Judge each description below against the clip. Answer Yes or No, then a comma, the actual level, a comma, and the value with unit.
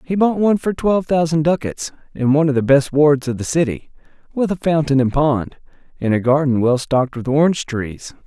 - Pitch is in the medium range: Yes, medium, 145 Hz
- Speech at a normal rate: No, fast, 210 wpm